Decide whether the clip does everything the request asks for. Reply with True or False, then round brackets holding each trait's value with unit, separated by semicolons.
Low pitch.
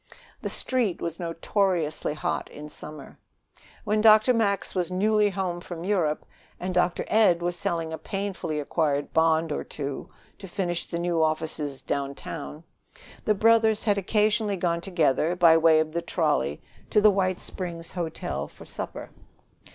False (175 Hz)